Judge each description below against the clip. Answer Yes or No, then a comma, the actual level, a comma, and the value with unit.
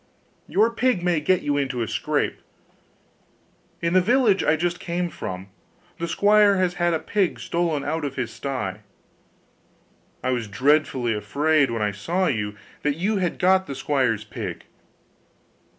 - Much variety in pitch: Yes, wide, 6.3 semitones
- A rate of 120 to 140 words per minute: No, average, 155 wpm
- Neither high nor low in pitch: Yes, medium, 155 Hz